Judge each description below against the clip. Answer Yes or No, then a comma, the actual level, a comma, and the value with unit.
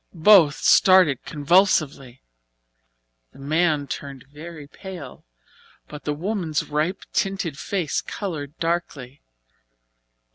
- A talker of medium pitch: Yes, medium, 155 Hz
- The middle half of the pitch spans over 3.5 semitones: Yes, average, 4.0 semitones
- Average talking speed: No, slow, 95 wpm